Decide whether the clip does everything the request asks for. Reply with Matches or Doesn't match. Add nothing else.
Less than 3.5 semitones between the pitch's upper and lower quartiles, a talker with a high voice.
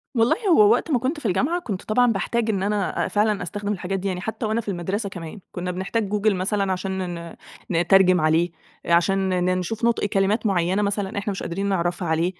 Matches